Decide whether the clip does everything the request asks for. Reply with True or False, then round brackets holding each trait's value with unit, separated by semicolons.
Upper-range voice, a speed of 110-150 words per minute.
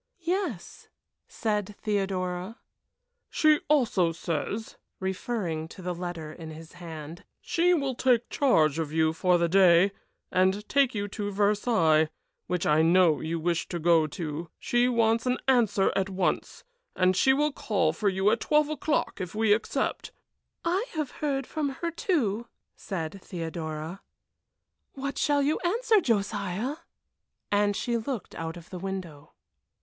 True (195 Hz; 145 wpm)